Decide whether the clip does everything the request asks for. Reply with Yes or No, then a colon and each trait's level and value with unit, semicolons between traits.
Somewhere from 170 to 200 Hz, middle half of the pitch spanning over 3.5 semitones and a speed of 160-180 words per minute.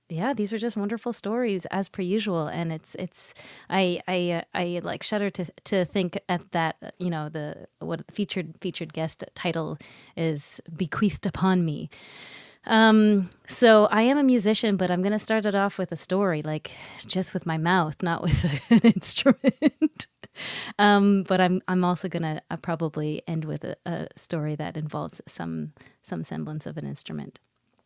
Yes: medium, 185 Hz; average, 3.9 semitones; average, 170 wpm